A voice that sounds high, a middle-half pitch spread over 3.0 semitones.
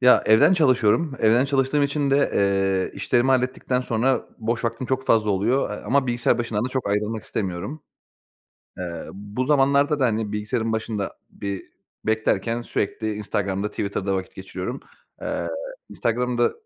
No: low, 115 Hz; average, 4.0 semitones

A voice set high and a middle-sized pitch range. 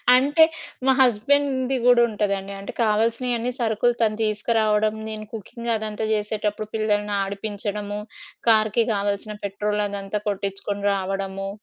No: high, 210 Hz; narrow, 2.0 semitones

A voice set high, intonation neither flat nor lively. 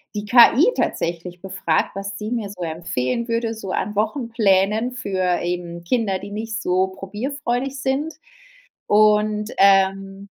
Yes: high, 205 Hz; average, 3.5 semitones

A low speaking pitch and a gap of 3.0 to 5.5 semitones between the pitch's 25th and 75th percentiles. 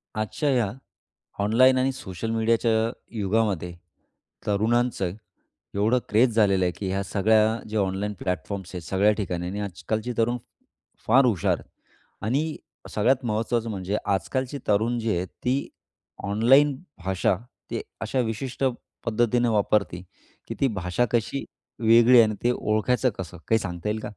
Yes: low, 110 Hz; average, 3.5 semitones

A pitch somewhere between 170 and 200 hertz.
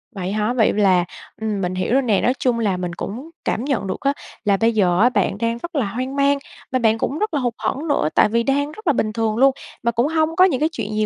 No: high, 235 Hz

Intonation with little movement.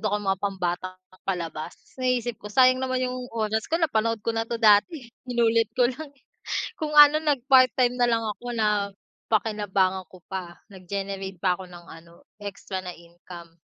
No: average, 4.7 semitones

